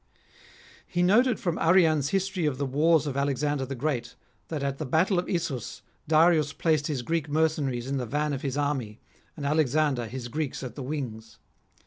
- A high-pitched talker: No, medium, 145 Hz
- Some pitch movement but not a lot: Yes, average, 3.3 semitones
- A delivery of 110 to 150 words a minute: No, average, 180 wpm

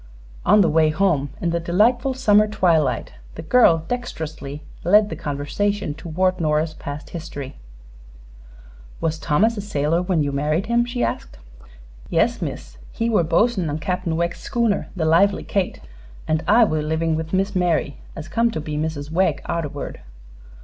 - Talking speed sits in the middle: Yes, average, 160 wpm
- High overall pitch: No, medium, 170 Hz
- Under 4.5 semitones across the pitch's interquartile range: No, average, 4.8 semitones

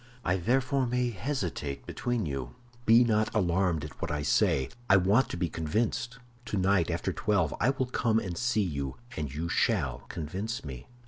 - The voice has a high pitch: No, very low, 95 Hz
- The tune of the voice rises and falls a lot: Yes, wide, 7.2 semitones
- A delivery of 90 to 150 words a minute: No, average, 175 wpm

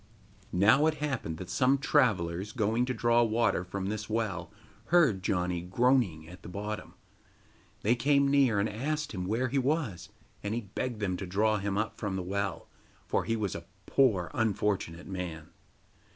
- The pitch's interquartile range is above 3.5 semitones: Yes, average, 5.1 semitones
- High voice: No, low, 105 Hz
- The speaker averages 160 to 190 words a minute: Yes, average, 170 wpm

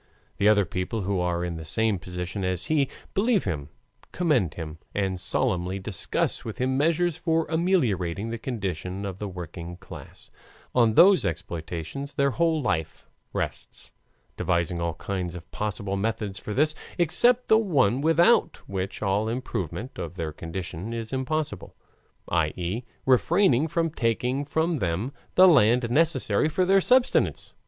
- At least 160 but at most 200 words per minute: No, average, 150 wpm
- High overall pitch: No, low, 110 Hz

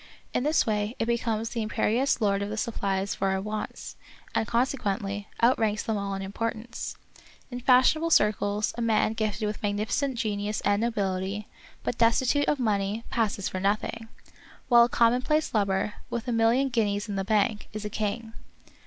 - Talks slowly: No, average, 170 wpm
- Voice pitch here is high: Yes, high, 215 Hz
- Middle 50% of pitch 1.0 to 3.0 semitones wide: Yes, narrow, 2.6 semitones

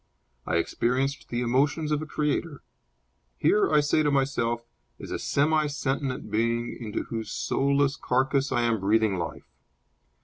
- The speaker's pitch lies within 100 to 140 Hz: Yes, low, 135 Hz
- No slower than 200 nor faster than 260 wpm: No, average, 145 wpm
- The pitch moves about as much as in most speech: Yes, average, 3.7 semitones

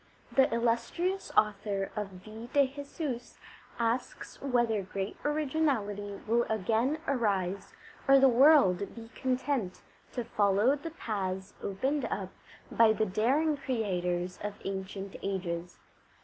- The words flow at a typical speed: No, slow, 120 wpm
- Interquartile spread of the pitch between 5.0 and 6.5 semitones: Yes, wide, 5.4 semitones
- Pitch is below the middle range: No, high, 225 Hz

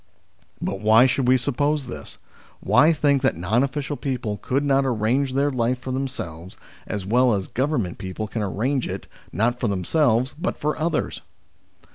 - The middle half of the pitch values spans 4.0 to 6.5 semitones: Yes, average, 4.4 semitones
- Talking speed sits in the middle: Yes, average, 165 wpm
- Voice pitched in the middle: No, low, 125 Hz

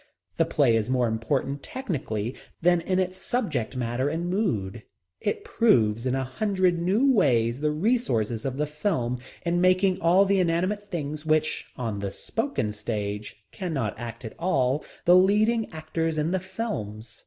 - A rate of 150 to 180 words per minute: Yes, average, 160 wpm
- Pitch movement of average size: No, wide, 7.9 semitones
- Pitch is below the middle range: No, medium, 155 Hz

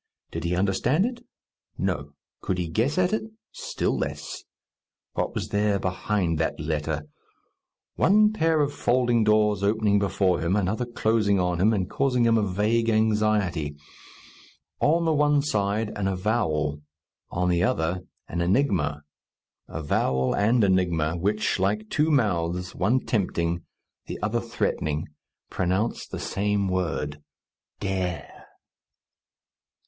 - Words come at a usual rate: No, slow, 130 wpm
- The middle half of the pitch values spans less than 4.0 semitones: No, average, 4.7 semitones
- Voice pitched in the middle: No, low, 100 Hz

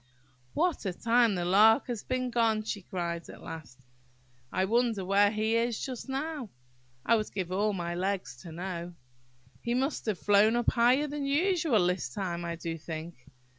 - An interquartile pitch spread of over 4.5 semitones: Yes, wide, 5.4 semitones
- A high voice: Yes, high, 210 Hz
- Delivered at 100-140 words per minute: No, average, 175 wpm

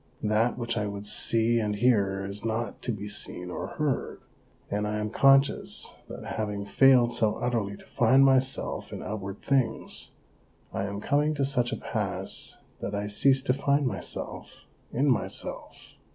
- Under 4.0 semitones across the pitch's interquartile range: No, average, 4.3 semitones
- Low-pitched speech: Yes, low, 115 Hz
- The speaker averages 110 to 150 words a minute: No, average, 165 wpm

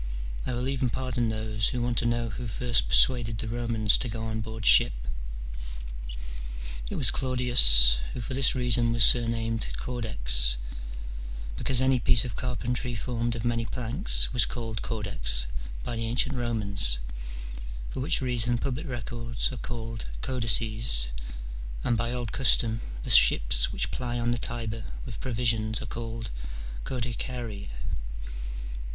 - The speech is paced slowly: No, average, 145 wpm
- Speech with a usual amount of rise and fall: No, narrow, 1.9 semitones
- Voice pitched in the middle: No, low, 115 Hz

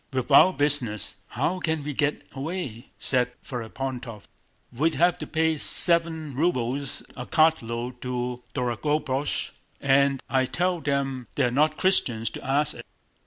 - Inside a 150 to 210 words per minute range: No, slow, 135 wpm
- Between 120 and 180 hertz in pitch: Yes, medium, 140 Hz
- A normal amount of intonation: Yes, average, 4.0 semitones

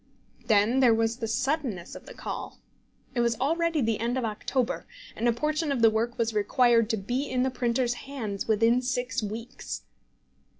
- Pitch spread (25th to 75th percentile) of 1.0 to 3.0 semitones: Yes, narrow, 2.5 semitones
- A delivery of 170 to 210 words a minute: Yes, average, 180 wpm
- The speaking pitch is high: Yes, high, 240 Hz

